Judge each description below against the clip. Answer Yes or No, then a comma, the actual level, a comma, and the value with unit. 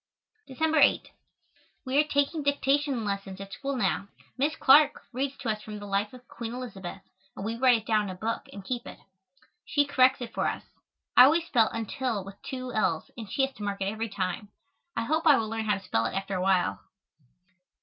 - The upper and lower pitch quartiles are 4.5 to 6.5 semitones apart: Yes, average, 5.2 semitones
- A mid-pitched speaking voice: No, high, 230 Hz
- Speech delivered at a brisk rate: Yes, fast, 215 wpm